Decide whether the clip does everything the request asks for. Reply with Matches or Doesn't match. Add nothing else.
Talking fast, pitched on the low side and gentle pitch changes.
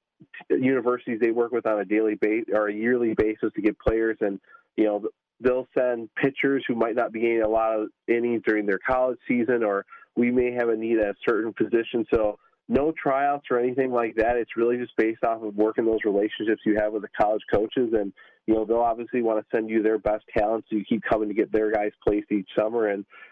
Matches